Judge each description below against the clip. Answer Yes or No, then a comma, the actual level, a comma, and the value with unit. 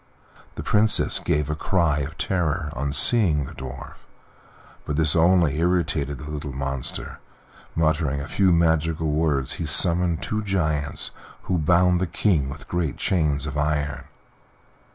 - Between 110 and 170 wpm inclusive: Yes, average, 145 wpm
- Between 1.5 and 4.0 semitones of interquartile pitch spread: Yes, average, 3.2 semitones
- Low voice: Yes, very low, 80 Hz